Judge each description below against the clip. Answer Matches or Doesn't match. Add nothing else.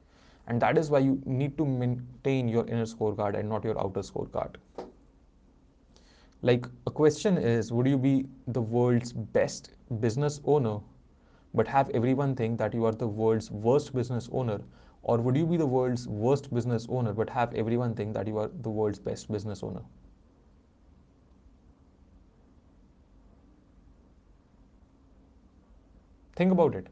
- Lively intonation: Matches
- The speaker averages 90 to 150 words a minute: Matches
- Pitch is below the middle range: Matches